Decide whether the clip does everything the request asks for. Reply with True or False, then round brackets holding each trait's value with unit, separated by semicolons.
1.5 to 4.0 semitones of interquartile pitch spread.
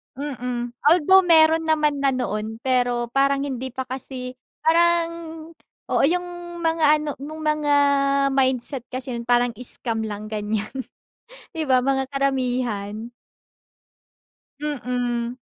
True (3.7 semitones)